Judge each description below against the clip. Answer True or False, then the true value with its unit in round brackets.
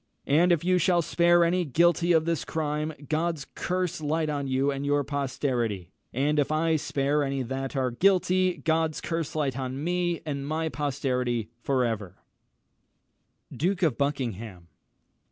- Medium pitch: True (150 Hz)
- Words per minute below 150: False (155 wpm)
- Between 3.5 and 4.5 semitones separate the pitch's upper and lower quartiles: True (3.9 semitones)